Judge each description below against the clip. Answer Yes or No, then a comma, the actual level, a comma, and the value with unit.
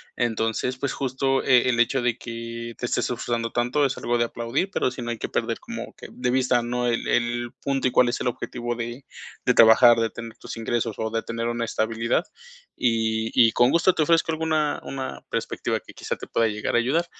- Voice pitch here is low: Yes, low, 120 Hz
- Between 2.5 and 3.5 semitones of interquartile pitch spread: No, narrow, 1.9 semitones